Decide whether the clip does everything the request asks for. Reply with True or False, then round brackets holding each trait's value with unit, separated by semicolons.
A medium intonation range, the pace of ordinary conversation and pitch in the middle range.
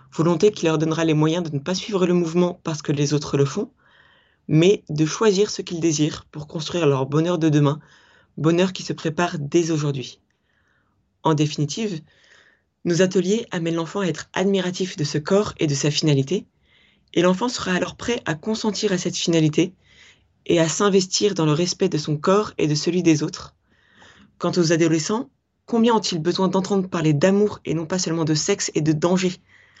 True (3.2 semitones; 190 wpm; 170 Hz)